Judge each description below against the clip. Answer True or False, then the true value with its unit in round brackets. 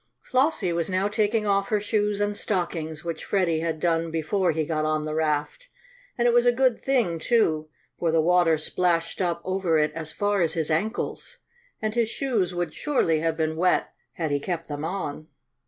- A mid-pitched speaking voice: True (175 Hz)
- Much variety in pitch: False (4.5 semitones)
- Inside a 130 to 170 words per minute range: False (195 wpm)